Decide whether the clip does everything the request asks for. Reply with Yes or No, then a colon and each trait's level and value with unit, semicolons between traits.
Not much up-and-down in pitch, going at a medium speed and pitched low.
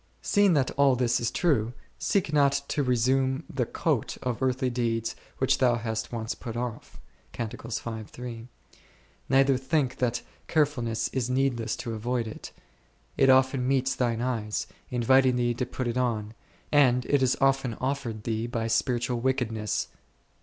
Yes: narrow, 2.3 semitones; average, 150 wpm; low, 125 Hz